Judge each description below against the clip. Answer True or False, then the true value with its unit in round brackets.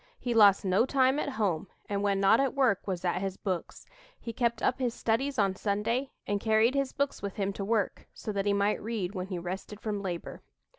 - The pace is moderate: False (225 wpm)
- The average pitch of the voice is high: True (205 Hz)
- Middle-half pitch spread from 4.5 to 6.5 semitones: False (3.3 semitones)